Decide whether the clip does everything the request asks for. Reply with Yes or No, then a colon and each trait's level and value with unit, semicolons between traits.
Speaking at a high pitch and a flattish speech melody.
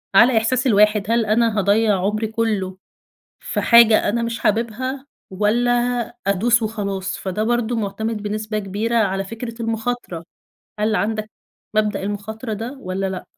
Yes: high, 215 Hz; narrow, 2.2 semitones